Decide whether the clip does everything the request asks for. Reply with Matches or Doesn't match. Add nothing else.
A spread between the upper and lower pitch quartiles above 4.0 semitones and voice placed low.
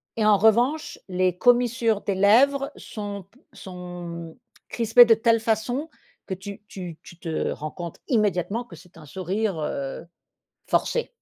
Doesn't match